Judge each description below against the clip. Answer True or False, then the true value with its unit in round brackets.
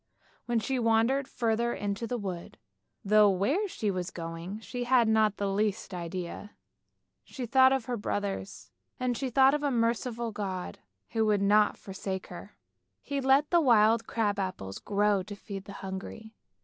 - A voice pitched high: True (215 Hz)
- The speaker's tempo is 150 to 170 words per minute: True (165 wpm)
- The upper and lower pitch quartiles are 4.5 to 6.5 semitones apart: False (3.7 semitones)